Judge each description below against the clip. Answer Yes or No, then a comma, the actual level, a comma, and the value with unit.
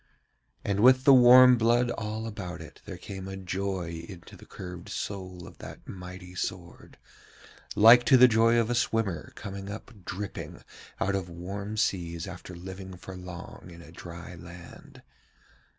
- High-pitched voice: No, very low, 95 Hz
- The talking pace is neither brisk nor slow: Yes, average, 160 wpm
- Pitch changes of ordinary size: Yes, average, 3.7 semitones